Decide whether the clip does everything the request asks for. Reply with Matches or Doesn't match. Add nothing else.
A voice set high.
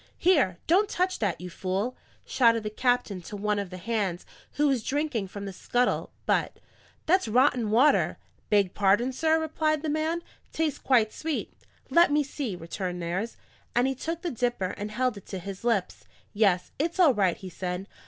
Matches